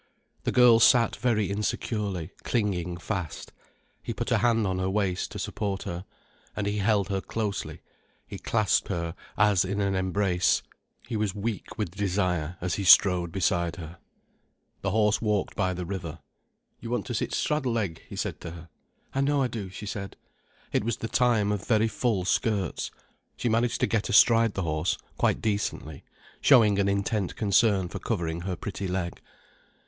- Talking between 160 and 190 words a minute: Yes, average, 175 wpm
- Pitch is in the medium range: No, low, 100 Hz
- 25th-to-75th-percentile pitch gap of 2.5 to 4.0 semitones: Yes, average, 3.3 semitones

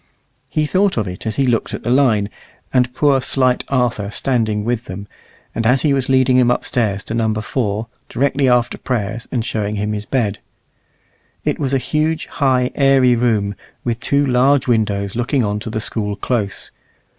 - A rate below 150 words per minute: No, average, 185 wpm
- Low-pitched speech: Yes, low, 120 Hz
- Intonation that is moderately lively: Yes, average, 3.7 semitones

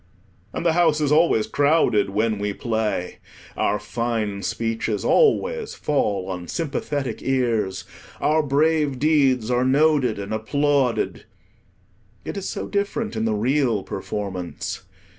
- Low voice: Yes, low, 125 Hz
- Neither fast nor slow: No, slow, 125 wpm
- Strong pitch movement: Yes, wide, 6.1 semitones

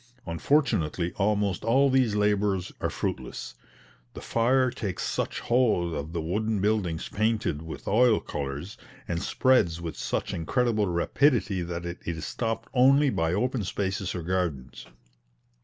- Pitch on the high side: No, low, 100 Hz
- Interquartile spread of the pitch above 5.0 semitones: Yes, wide, 5.4 semitones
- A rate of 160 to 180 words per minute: No, average, 140 wpm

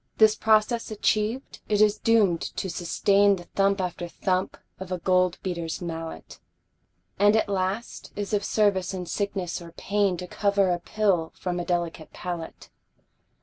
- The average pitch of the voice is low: No, high, 190 Hz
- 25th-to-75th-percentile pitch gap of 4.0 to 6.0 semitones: No, average, 2.8 semitones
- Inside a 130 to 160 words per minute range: Yes, average, 155 wpm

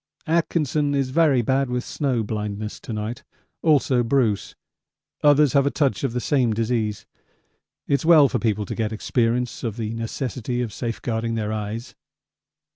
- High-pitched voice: No, low, 120 Hz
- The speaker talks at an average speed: Yes, average, 155 wpm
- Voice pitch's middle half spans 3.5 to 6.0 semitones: Yes, average, 3.8 semitones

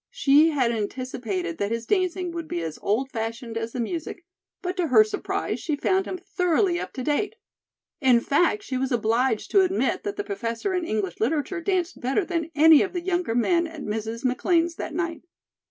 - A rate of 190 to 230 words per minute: Yes, average, 195 wpm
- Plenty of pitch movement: Yes, wide, 7.4 semitones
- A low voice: No, very high, 295 Hz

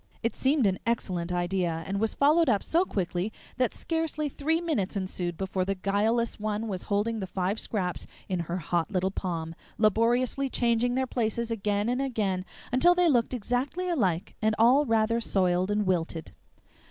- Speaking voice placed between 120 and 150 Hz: No, high, 215 Hz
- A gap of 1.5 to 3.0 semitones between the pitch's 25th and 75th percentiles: No, average, 4.9 semitones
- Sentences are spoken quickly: No, average, 170 wpm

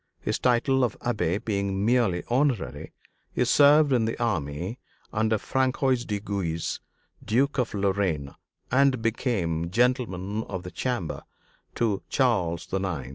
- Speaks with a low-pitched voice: Yes, low, 110 Hz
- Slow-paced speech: Yes, slow, 130 wpm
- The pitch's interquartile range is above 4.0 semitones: Yes, average, 5.2 semitones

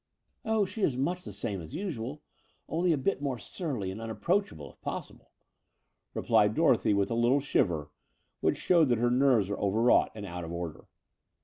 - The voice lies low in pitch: Yes, low, 120 Hz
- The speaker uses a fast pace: No, average, 180 wpm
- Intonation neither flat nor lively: No, wide, 7.9 semitones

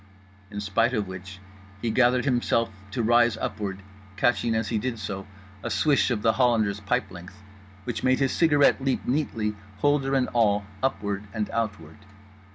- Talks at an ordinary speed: Yes, average, 165 wpm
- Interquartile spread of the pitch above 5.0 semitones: No, average, 3.5 semitones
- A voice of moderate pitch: No, low, 110 Hz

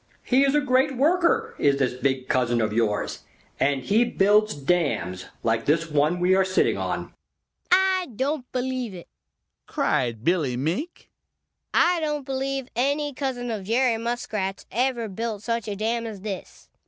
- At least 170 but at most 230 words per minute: No, average, 155 wpm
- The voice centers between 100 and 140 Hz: No, high, 220 Hz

